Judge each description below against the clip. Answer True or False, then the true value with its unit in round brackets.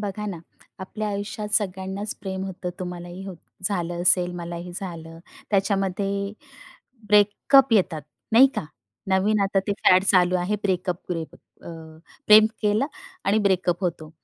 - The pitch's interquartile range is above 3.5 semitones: False (2.5 semitones)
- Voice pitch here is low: False (190 Hz)